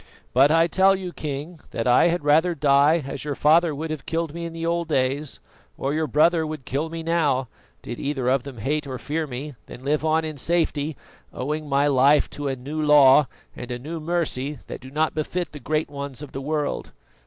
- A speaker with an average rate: No, fast, 215 wpm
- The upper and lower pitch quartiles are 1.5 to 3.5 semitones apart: Yes, average, 2.7 semitones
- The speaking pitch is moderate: Yes, medium, 150 Hz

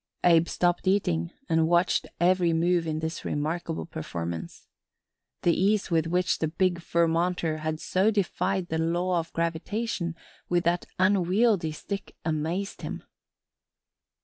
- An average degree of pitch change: No, narrow, 2.3 semitones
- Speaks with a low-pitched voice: No, medium, 170 Hz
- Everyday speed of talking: No, slow, 130 wpm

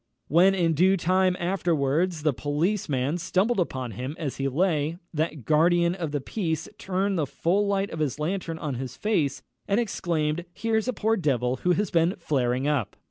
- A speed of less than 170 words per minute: No, average, 180 wpm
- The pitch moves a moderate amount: Yes, average, 4.5 semitones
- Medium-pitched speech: Yes, medium, 165 Hz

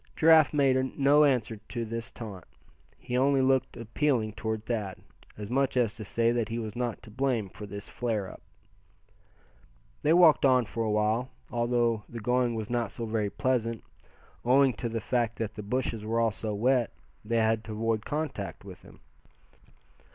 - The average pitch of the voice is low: Yes, low, 115 Hz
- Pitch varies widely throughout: No, average, 2.8 semitones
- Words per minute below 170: No, average, 180 wpm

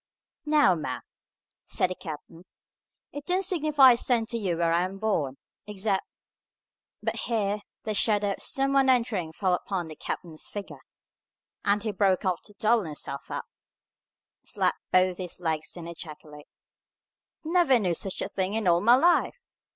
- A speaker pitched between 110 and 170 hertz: No, high, 195 Hz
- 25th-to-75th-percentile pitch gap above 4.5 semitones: Yes, average, 5.2 semitones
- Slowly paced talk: No, average, 165 wpm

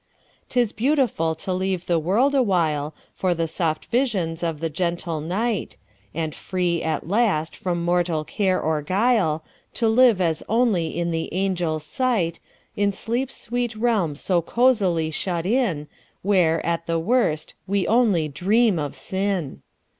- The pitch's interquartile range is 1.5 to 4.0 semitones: No, average, 5.2 semitones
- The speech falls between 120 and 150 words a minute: Yes, slow, 135 wpm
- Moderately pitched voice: Yes, medium, 180 Hz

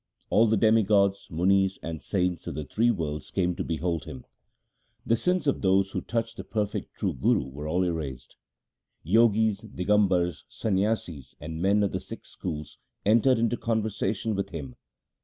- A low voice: Yes, very low, 95 Hz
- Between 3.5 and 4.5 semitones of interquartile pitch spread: No, average, 5.0 semitones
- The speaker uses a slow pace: No, average, 160 wpm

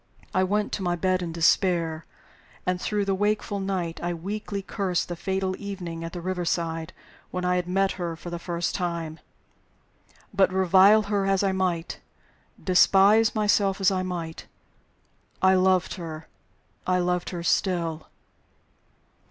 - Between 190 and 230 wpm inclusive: No, average, 150 wpm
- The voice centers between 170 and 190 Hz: Yes, medium, 185 Hz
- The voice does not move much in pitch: Yes, narrow, 2.2 semitones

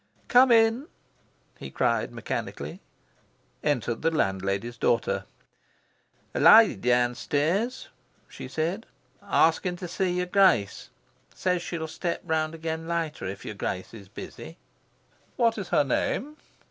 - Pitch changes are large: Yes, wide, 7.4 semitones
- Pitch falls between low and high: Yes, medium, 160 Hz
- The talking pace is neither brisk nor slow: No, slow, 120 wpm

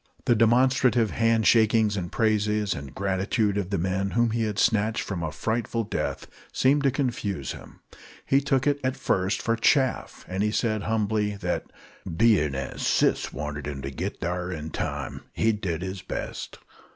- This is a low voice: Yes, low, 105 Hz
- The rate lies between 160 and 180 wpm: Yes, average, 170 wpm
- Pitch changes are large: No, average, 3.9 semitones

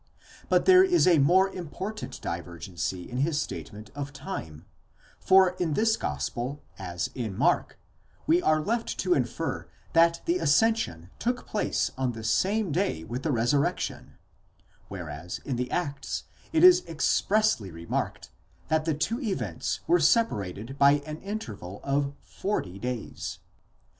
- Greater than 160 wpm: No, average, 145 wpm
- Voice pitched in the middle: Yes, medium, 145 Hz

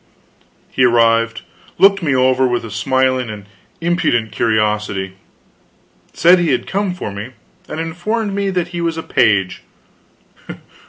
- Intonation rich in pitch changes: Yes, wide, 7.6 semitones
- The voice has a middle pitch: No, low, 130 Hz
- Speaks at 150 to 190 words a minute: No, average, 140 wpm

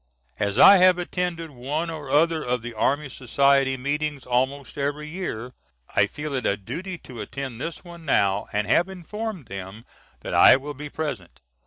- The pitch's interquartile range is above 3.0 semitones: Yes, average, 5.0 semitones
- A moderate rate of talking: Yes, average, 175 wpm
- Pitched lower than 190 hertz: Yes, medium, 140 Hz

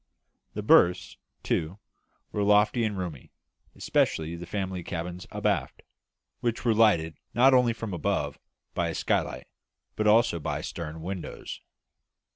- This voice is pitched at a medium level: No, very low, 95 Hz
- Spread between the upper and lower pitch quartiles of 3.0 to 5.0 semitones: Yes, average, 4.4 semitones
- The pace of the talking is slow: Yes, slow, 130 wpm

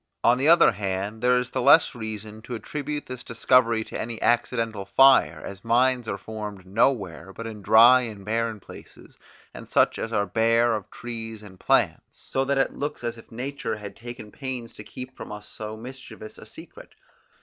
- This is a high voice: No, low, 115 Hz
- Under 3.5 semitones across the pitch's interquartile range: Yes, average, 2.9 semitones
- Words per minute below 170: No, average, 190 wpm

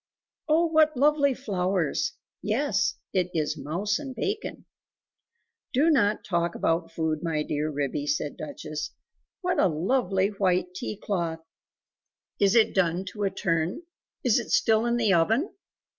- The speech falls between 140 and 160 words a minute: Yes, average, 145 wpm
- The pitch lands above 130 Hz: Yes, high, 190 Hz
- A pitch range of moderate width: No, wide, 6.6 semitones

